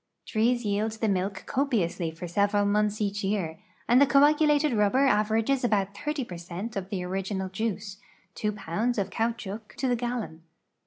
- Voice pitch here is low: No, high, 210 Hz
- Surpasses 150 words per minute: Yes, average, 165 wpm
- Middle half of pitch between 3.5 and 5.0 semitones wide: Yes, average, 3.8 semitones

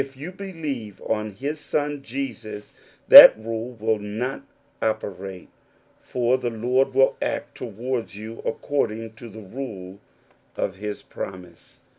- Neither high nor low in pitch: No, low, 115 Hz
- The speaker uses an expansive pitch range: No, average, 3.9 semitones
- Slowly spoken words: Yes, slow, 125 wpm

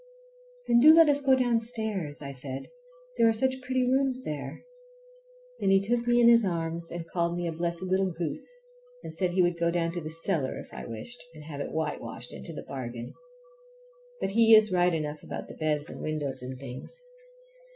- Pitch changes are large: Yes, wide, 7.3 semitones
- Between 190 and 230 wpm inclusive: Yes, average, 195 wpm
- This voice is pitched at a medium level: Yes, medium, 175 Hz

